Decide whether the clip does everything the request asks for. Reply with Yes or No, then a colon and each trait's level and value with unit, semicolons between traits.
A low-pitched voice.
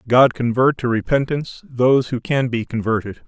Yes: low, 125 Hz